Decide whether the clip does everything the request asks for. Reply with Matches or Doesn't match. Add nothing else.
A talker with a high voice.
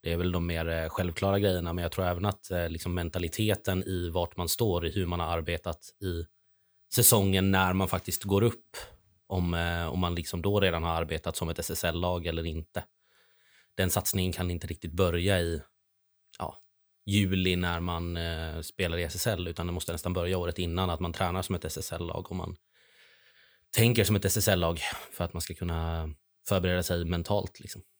Doesn't match